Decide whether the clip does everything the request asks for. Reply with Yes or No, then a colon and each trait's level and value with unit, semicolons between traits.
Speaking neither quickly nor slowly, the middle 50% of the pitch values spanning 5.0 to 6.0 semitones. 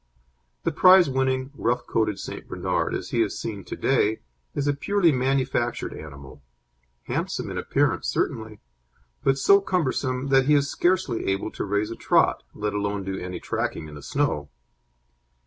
Yes: average, 160 wpm; wide, 5.5 semitones